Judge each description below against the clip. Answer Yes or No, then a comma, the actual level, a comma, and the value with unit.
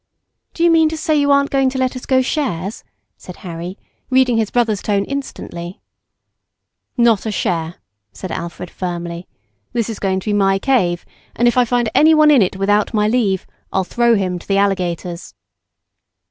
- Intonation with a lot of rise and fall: Yes, wide, 5.8 semitones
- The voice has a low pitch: No, high, 210 Hz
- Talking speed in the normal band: Yes, average, 180 wpm